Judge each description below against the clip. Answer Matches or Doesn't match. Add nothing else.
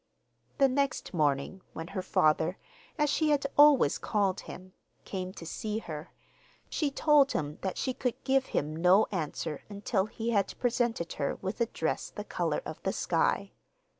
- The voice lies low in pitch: Doesn't match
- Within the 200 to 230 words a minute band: Doesn't match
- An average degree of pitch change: Doesn't match